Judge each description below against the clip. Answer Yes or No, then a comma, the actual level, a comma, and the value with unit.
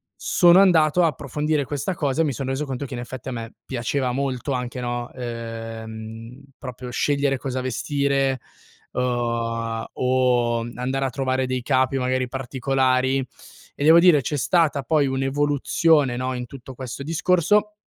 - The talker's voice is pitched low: Yes, low, 130 Hz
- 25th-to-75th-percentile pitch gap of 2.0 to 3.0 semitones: Yes, narrow, 2.5 semitones